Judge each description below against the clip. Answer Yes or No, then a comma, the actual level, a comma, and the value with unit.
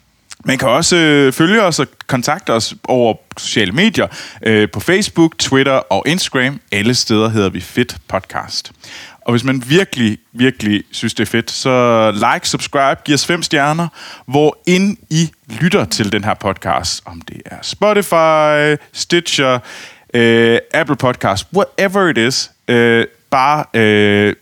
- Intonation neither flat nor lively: No, wide, 5.9 semitones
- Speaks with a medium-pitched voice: No, low, 130 Hz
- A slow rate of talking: Yes, slow, 140 wpm